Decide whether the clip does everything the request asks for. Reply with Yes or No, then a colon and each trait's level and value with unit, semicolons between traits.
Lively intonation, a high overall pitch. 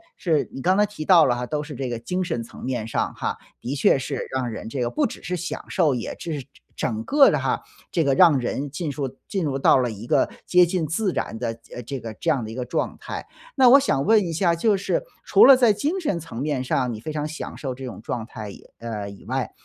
No: wide, 6.4 semitones; medium, 140 Hz